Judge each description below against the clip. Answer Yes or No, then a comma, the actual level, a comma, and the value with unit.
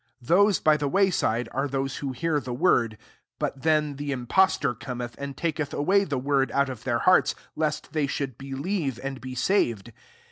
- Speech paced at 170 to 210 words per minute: Yes, average, 190 wpm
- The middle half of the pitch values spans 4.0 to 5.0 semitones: No, average, 3.5 semitones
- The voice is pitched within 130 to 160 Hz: Yes, medium, 140 Hz